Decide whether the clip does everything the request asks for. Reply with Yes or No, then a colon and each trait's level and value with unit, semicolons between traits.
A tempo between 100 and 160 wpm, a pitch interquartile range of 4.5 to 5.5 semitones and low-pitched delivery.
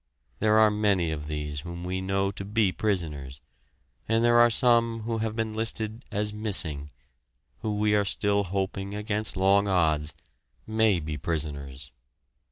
Yes: average, 155 wpm; average, 4.9 semitones; low, 100 Hz